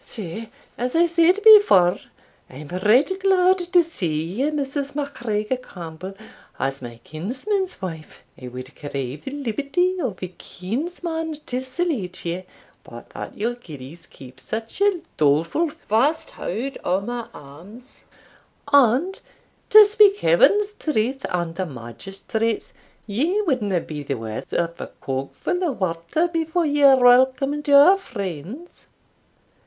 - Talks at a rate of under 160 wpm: Yes, slow, 135 wpm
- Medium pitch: No, high, 240 Hz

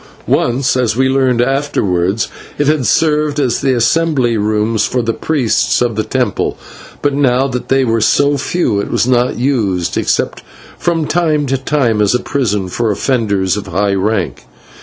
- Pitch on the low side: Yes, low, 125 Hz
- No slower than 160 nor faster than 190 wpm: Yes, average, 170 wpm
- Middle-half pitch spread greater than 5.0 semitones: No, average, 4.6 semitones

